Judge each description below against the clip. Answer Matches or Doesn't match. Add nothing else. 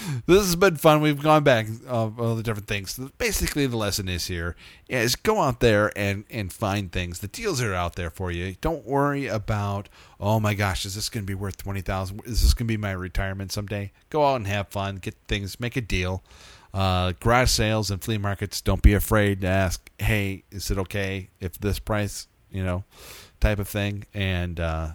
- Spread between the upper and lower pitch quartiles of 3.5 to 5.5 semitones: Doesn't match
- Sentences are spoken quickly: Matches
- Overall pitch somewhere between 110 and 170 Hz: Doesn't match